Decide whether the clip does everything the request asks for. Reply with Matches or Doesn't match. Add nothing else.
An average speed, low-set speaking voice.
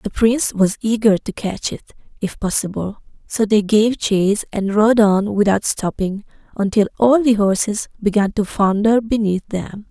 Doesn't match